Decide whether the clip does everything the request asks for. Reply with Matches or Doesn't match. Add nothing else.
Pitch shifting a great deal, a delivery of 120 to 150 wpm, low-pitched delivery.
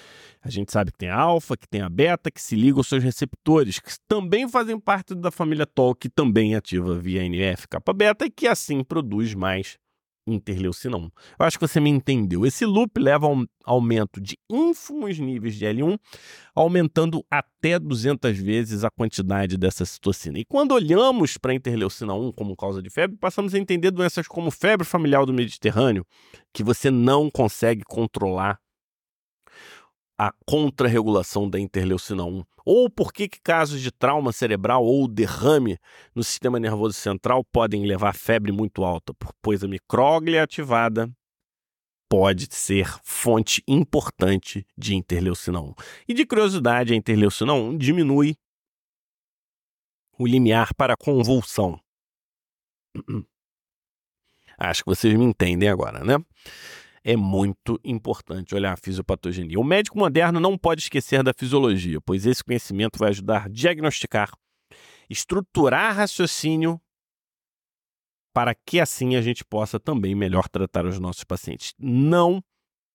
Matches